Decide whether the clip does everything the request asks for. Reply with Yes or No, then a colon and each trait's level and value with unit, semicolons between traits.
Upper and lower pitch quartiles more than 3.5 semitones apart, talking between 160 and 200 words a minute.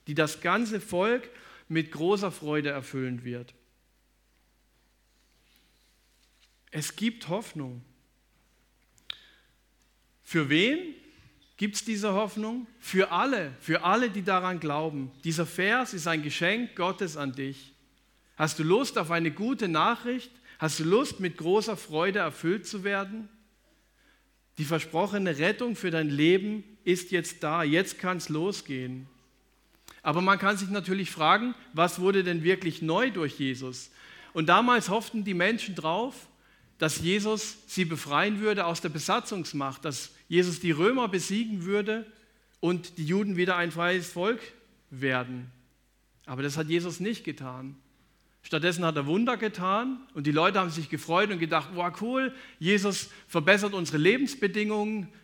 No: average, 5.2 semitones; average, 140 wpm